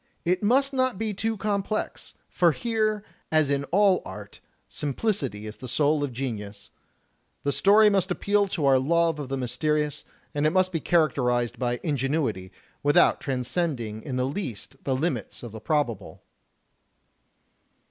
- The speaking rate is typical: Yes, average, 155 wpm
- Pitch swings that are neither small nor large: No, wide, 6.8 semitones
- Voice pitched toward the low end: No, medium, 150 Hz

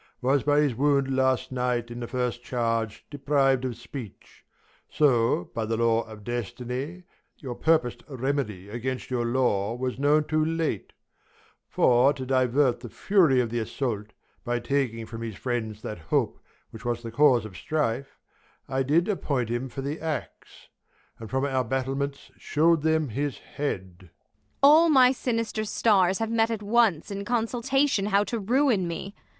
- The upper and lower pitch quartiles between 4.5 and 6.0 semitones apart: Yes, average, 5.0 semitones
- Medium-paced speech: Yes, average, 165 wpm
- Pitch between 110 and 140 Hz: Yes, low, 135 Hz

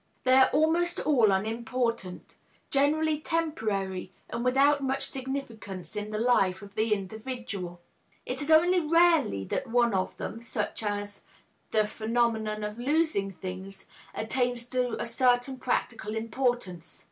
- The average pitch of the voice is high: Yes, high, 235 Hz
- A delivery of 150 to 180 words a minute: No, slow, 135 wpm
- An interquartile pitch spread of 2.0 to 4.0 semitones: No, average, 4.6 semitones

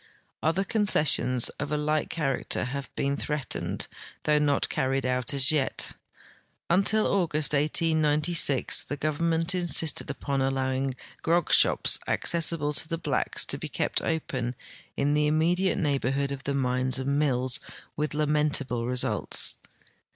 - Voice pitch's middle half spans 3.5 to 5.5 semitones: No, average, 2.9 semitones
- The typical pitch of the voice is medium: Yes, medium, 150 Hz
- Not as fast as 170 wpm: Yes, slow, 135 wpm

